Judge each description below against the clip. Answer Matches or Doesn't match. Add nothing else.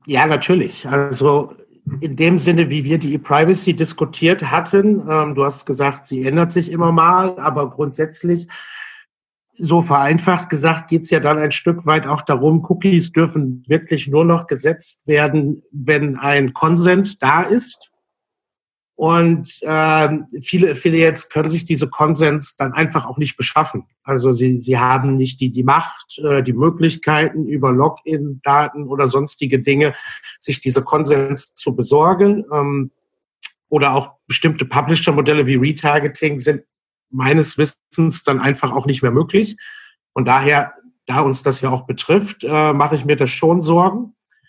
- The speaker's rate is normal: Matches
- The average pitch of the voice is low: Doesn't match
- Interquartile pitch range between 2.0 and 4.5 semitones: Matches